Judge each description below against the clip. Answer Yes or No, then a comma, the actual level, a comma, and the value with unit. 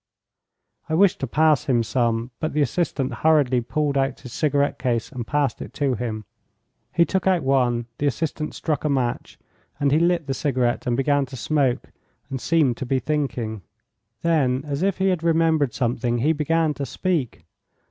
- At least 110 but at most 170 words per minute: No, average, 180 wpm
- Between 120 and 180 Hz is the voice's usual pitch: Yes, medium, 140 Hz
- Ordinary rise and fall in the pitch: Yes, average, 4.0 semitones